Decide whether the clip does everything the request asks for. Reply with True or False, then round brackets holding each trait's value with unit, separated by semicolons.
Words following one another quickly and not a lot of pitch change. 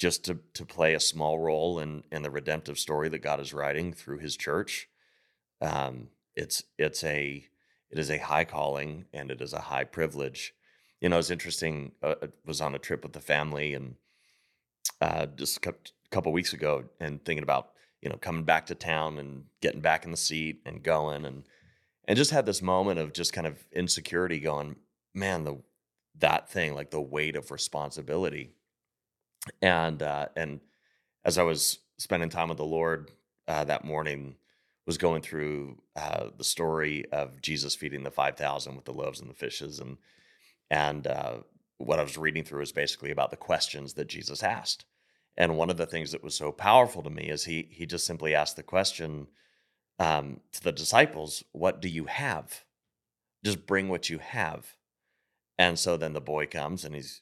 False (190 wpm; 2.2 semitones)